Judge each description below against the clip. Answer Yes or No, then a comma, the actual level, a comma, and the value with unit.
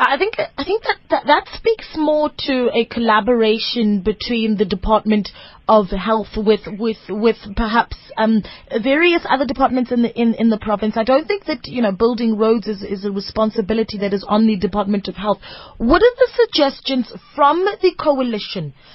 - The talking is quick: No, average, 180 wpm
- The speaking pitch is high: Yes, high, 225 Hz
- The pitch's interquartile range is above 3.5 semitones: Yes, average, 4.6 semitones